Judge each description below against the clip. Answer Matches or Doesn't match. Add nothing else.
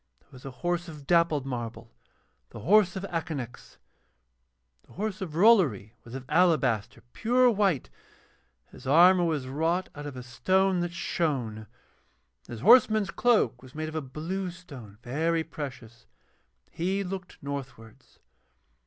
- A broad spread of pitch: Matches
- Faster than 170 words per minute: Doesn't match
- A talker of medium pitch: Matches